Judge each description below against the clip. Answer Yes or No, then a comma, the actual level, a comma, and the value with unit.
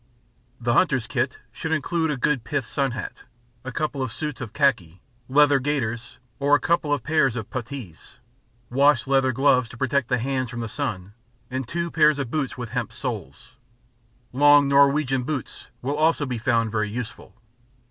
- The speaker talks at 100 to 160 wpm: No, average, 170 wpm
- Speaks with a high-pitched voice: No, low, 135 Hz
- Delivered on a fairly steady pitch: No, average, 3.3 semitones